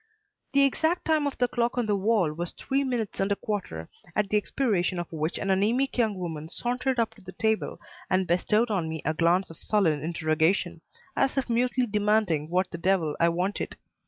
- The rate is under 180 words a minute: No, average, 200 wpm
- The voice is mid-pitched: No, high, 200 Hz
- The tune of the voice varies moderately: No, wide, 5.7 semitones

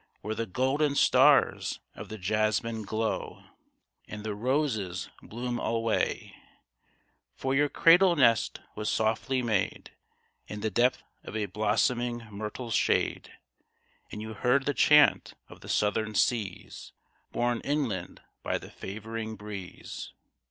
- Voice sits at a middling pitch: No, low, 110 Hz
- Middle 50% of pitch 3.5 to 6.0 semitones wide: No, average, 2.9 semitones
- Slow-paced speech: Yes, slow, 125 wpm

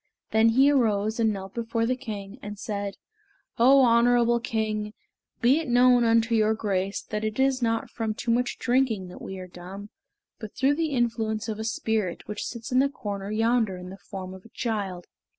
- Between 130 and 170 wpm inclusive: No, average, 195 wpm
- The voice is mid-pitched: No, high, 225 Hz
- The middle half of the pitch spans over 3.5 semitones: No, average, 2.8 semitones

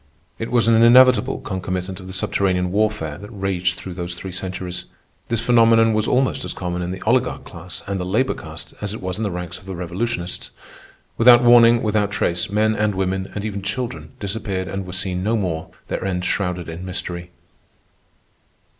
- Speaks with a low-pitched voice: Yes, very low, 95 Hz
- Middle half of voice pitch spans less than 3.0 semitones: No, average, 3.4 semitones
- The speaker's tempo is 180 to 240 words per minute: Yes, average, 190 wpm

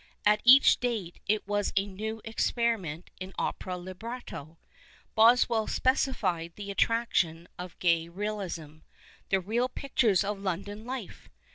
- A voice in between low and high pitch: No, high, 205 Hz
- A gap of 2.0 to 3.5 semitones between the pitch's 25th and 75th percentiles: No, average, 4.2 semitones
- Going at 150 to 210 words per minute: No, slow, 135 wpm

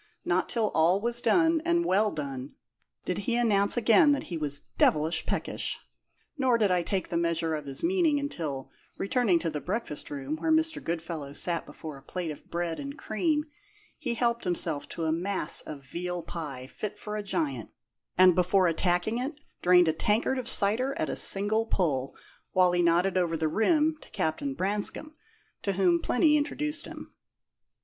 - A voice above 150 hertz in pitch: Yes, medium, 185 Hz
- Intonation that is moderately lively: No, wide, 6.5 semitones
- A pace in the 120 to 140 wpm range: No, average, 180 wpm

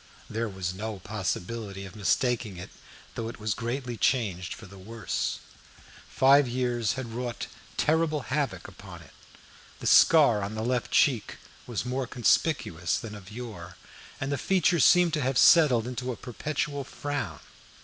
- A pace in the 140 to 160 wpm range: Yes, average, 155 wpm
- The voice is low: Yes, low, 120 Hz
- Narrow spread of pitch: No, average, 4.3 semitones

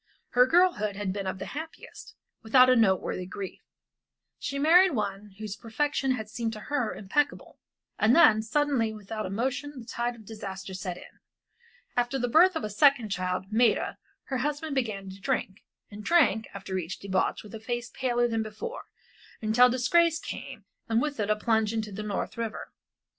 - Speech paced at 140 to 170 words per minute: No, average, 180 wpm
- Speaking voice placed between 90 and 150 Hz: No, high, 225 Hz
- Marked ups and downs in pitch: No, average, 4.3 semitones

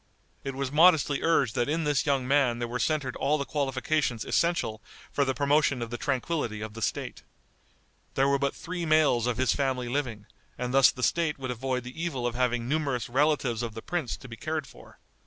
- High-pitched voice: No, low, 135 Hz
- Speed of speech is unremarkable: No, fast, 210 wpm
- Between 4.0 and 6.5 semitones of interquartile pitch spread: No, average, 3.4 semitones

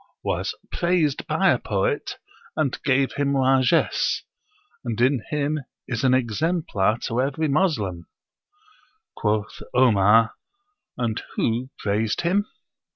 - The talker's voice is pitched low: Yes, low, 130 Hz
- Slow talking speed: Yes, slow, 115 wpm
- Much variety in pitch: No, average, 5.0 semitones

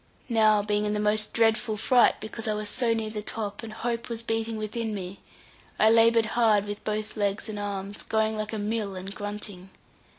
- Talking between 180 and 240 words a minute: Yes, average, 200 wpm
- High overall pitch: Yes, high, 215 Hz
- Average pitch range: No, narrow, 1.4 semitones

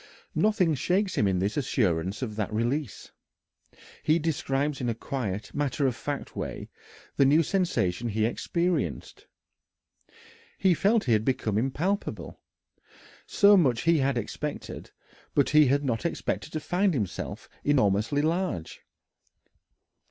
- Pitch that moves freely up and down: Yes, wide, 6.8 semitones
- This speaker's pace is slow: Yes, slow, 130 wpm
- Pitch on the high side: No, medium, 140 Hz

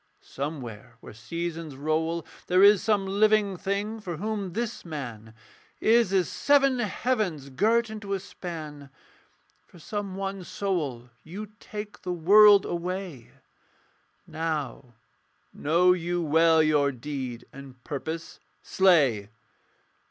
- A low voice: No, medium, 175 Hz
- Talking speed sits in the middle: No, slow, 115 wpm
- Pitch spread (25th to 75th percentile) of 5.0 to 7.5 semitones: Yes, wide, 5.4 semitones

